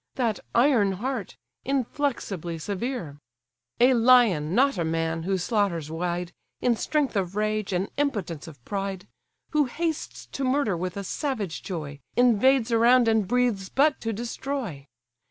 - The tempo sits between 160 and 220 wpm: No, average, 140 wpm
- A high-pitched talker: Yes, high, 215 Hz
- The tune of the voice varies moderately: No, wide, 6.2 semitones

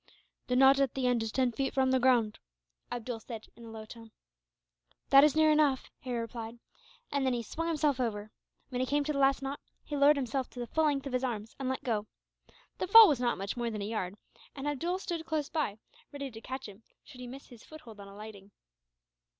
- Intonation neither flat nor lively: Yes, average, 3.8 semitones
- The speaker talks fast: Yes, fast, 230 wpm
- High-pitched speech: Yes, very high, 255 Hz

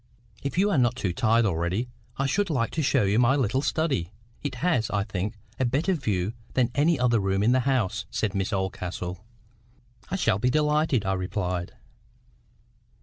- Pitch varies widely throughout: Yes, wide, 6.1 semitones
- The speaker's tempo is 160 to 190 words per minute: Yes, average, 180 wpm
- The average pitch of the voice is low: Yes, low, 120 Hz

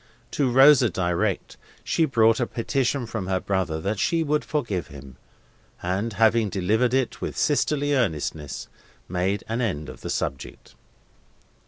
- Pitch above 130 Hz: No, low, 110 Hz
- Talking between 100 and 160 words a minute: Yes, average, 145 wpm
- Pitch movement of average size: No, wide, 6.3 semitones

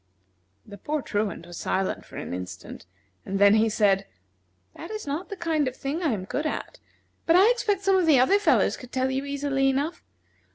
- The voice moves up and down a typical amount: No, wide, 8.1 semitones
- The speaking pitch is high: Yes, very high, 275 Hz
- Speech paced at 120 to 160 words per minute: No, fast, 205 wpm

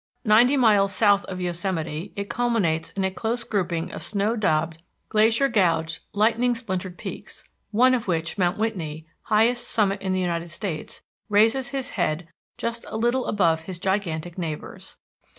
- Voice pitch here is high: Yes, high, 195 Hz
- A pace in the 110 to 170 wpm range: Yes, average, 155 wpm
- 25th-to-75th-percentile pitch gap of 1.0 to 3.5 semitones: No, average, 4.7 semitones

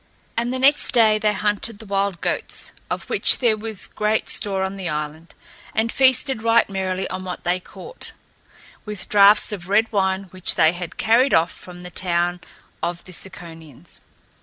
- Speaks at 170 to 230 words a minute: Yes, average, 175 wpm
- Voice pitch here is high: Yes, high, 195 Hz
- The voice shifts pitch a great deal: No, average, 3.6 semitones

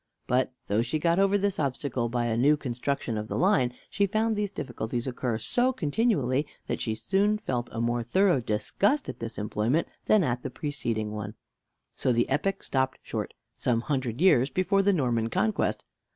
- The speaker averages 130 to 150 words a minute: No, average, 180 wpm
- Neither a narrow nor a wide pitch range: No, wide, 8.2 semitones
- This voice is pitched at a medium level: No, low, 130 Hz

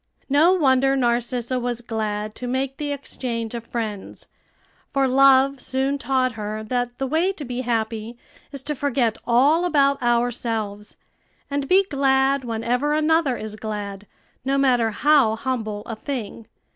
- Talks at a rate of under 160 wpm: Yes, average, 145 wpm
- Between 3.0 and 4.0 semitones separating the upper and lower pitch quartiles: Yes, average, 3.4 semitones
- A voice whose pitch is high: Yes, very high, 250 Hz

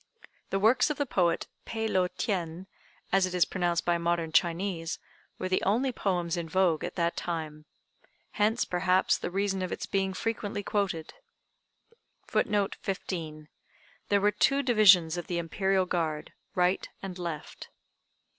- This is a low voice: No, medium, 185 Hz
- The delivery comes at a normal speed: Yes, average, 150 wpm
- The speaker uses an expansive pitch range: No, average, 2.9 semitones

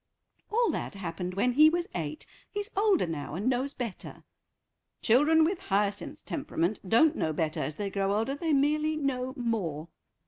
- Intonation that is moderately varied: No, wide, 8.5 semitones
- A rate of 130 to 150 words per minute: No, average, 165 wpm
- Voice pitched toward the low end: No, high, 245 Hz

